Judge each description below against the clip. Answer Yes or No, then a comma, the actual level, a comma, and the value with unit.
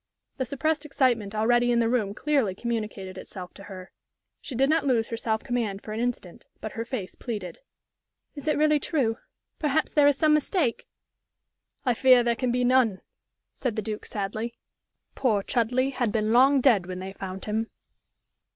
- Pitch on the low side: No, high, 235 Hz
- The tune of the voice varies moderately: Yes, average, 3.8 semitones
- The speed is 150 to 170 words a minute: No, average, 180 wpm